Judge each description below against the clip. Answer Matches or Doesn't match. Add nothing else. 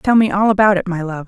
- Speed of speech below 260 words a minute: Doesn't match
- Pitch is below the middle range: Doesn't match